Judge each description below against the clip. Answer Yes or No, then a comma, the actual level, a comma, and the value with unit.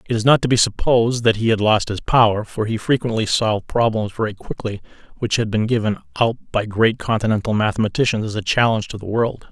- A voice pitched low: Yes, low, 110 Hz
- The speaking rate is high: Yes, fast, 215 wpm